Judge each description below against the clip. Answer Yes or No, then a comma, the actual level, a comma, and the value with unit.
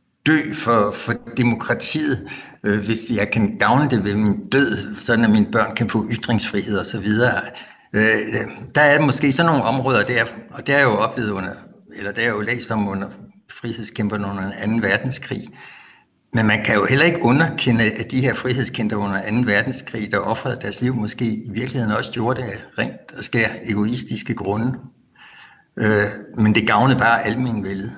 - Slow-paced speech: No, average, 180 wpm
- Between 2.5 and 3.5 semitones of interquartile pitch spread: Yes, average, 2.8 semitones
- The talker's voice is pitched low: Yes, low, 115 Hz